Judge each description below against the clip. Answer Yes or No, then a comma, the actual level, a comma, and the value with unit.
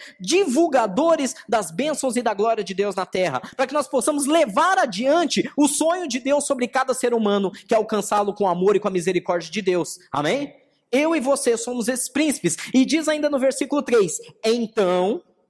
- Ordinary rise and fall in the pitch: No, wide, 6.3 semitones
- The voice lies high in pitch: Yes, very high, 250 Hz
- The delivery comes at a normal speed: No, fast, 195 wpm